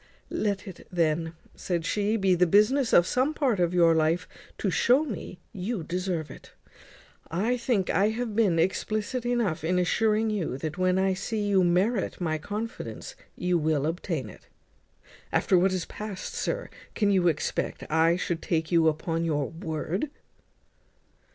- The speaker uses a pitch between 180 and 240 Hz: Yes, medium, 185 Hz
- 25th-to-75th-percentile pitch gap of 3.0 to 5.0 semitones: Yes, average, 4.2 semitones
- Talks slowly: No, average, 160 wpm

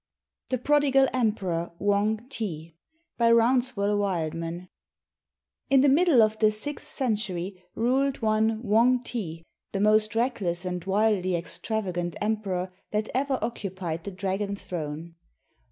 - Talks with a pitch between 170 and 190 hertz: No, high, 210 Hz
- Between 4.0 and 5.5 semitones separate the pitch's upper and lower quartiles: Yes, average, 4.5 semitones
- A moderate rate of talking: No, slow, 120 wpm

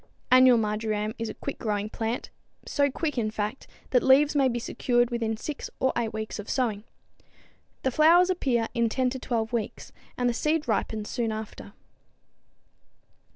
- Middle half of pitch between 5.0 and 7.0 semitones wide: No, average, 3.3 semitones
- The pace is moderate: Yes, average, 165 wpm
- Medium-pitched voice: No, high, 235 Hz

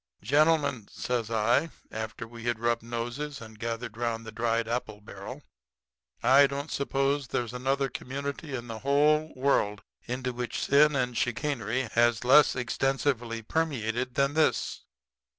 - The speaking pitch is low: Yes, low, 125 Hz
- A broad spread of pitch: No, average, 3.3 semitones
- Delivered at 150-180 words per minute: No, average, 140 wpm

